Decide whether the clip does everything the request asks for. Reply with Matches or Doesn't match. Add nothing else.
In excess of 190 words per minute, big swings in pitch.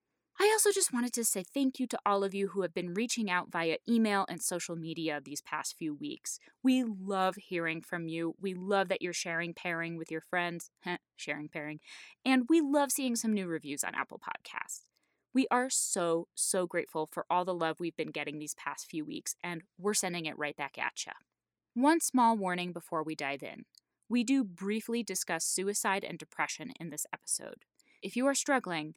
Matches